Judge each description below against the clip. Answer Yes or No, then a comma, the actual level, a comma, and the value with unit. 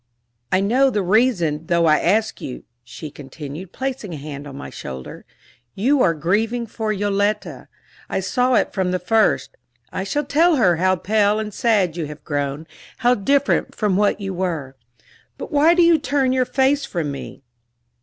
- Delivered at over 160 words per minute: Yes, average, 175 wpm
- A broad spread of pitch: Yes, wide, 7.1 semitones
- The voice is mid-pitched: No, high, 200 Hz